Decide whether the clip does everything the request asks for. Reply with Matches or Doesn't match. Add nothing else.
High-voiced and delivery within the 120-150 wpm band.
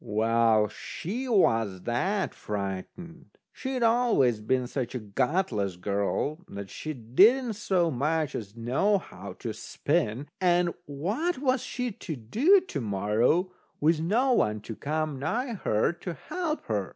Doesn't match